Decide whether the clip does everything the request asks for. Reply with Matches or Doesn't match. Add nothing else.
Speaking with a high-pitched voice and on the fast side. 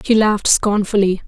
Doesn't match